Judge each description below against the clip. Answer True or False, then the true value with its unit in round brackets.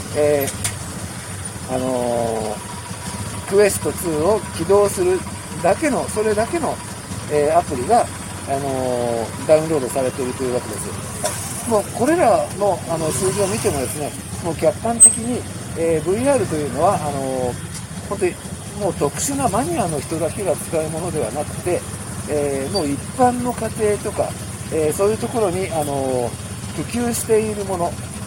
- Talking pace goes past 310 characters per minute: False (300 characters per minute)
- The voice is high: False (135 Hz)